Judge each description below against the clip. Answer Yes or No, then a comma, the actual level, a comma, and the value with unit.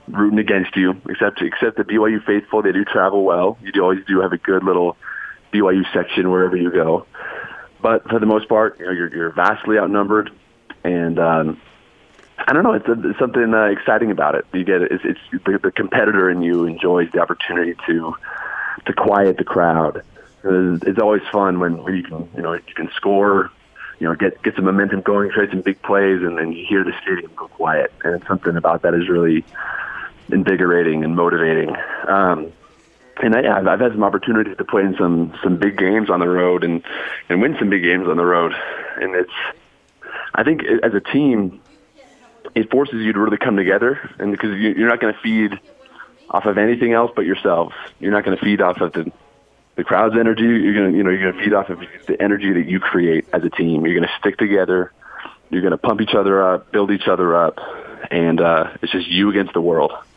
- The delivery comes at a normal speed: No, fast, 215 wpm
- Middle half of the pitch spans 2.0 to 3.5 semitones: Yes, average, 2.9 semitones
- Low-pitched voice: Yes, very low, 95 Hz